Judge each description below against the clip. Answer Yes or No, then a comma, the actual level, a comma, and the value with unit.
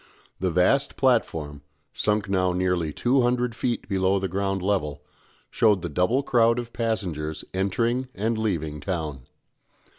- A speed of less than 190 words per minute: Yes, average, 140 wpm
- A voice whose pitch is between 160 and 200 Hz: No, very low, 95 Hz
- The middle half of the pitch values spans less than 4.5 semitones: No, average, 5.0 semitones